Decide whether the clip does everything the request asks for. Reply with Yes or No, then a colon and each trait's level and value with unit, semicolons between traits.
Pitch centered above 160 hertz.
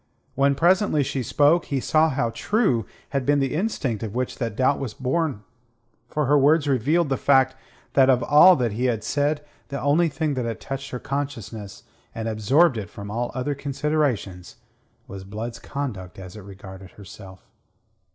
No: low, 135 Hz